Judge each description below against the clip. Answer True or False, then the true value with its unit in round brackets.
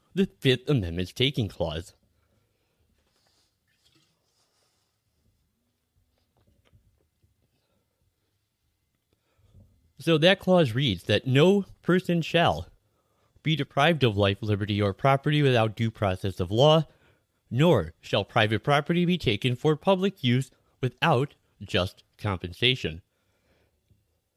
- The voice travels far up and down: True (6.2 semitones)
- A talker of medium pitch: False (110 Hz)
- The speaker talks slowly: True (90 wpm)